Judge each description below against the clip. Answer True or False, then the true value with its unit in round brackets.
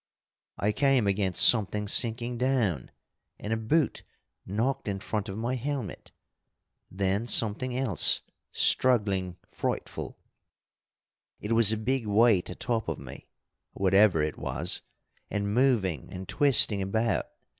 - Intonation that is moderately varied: True (3.8 semitones)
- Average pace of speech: False (125 wpm)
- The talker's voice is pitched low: True (110 Hz)